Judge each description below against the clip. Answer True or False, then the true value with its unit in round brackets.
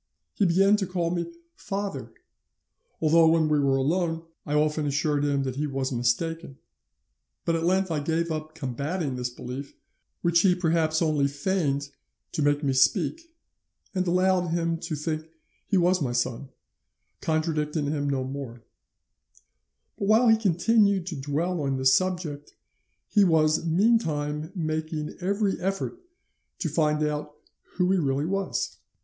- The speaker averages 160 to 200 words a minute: False (150 wpm)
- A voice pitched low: False (160 Hz)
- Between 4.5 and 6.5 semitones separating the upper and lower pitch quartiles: False (3.9 semitones)